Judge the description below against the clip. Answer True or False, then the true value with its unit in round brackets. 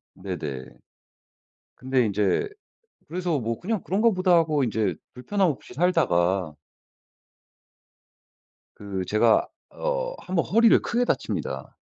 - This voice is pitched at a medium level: True (145 Hz)